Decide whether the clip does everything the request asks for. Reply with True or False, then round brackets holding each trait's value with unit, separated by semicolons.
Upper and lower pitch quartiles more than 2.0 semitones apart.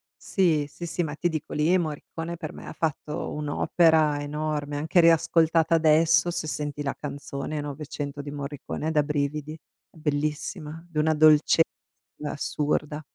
False (1.6 semitones)